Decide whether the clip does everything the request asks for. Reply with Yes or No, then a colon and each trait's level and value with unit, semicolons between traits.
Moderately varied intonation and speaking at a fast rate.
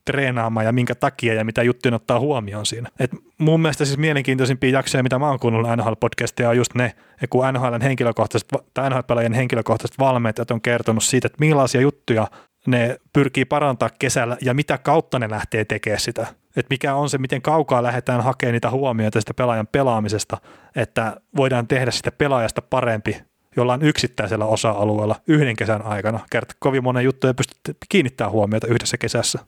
Yes: average, 3.0 semitones; fast, 170 wpm